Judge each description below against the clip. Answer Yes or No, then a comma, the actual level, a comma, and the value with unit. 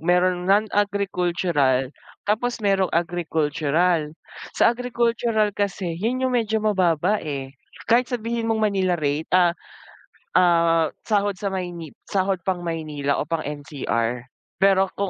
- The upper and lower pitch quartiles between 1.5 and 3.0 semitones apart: No, average, 4.5 semitones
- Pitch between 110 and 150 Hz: No, medium, 185 Hz